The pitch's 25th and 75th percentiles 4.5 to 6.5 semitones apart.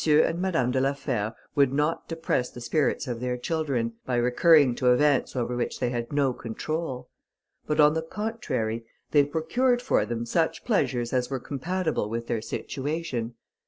Yes: average, 4.8 semitones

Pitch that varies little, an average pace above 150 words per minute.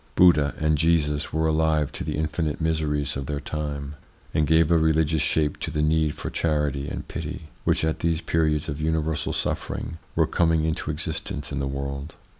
Yes: narrow, 1.6 semitones; average, 185 wpm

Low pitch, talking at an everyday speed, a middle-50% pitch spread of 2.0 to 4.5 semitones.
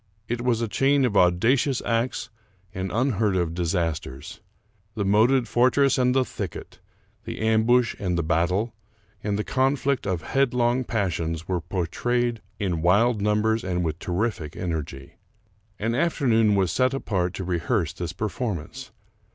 No: low, 105 Hz; average, 145 wpm; wide, 5.6 semitones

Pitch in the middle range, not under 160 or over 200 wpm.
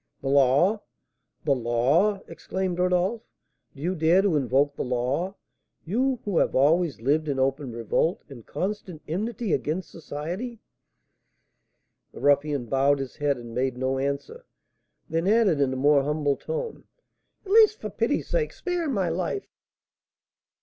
No: medium, 155 Hz; average, 145 wpm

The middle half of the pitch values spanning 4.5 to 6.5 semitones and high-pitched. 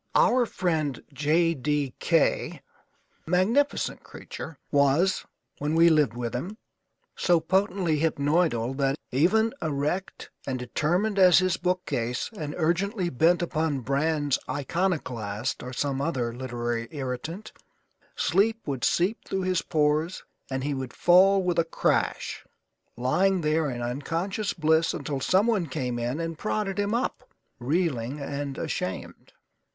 No: average, 5.2 semitones; medium, 155 Hz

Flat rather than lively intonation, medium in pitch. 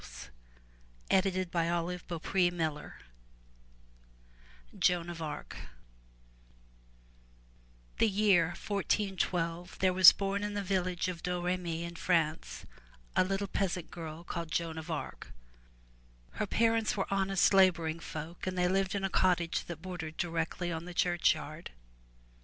Yes: narrow, 2.2 semitones; medium, 175 Hz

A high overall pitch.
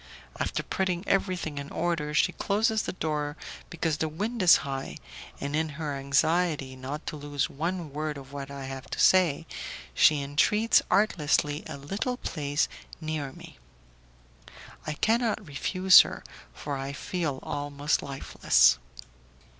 No: medium, 150 Hz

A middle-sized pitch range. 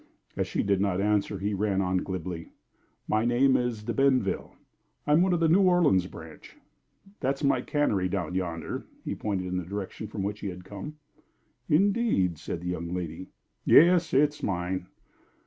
No: wide, 7.1 semitones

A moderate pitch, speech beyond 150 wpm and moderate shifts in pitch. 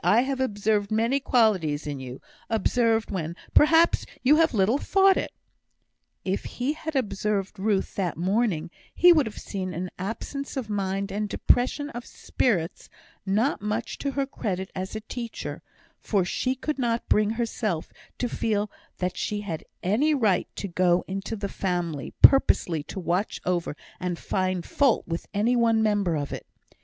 No: high, 210 Hz; average, 165 wpm; average, 4.8 semitones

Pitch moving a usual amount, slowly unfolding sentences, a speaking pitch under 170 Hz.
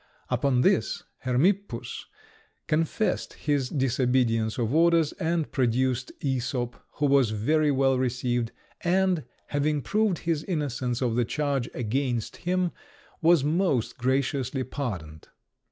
Yes: average, 4.0 semitones; slow, 115 wpm; low, 135 Hz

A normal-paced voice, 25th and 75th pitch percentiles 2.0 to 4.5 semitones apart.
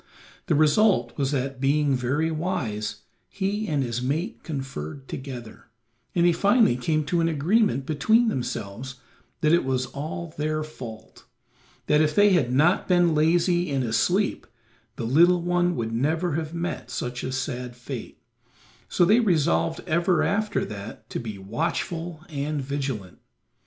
No: average, 150 wpm; average, 5.1 semitones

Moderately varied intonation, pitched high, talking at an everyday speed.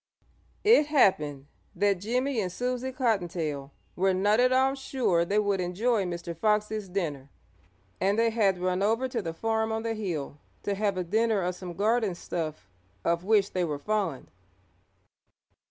Yes: average, 4.4 semitones; high, 200 Hz; average, 160 wpm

